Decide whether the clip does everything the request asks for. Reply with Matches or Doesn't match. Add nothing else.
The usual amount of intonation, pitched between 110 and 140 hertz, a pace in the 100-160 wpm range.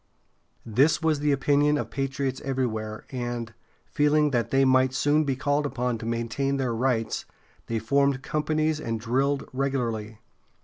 Matches